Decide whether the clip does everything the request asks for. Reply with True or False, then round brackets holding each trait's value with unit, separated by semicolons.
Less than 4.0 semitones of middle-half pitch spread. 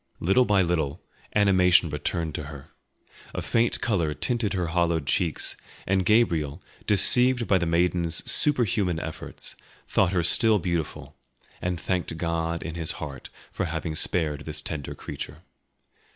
True (3.3 semitones)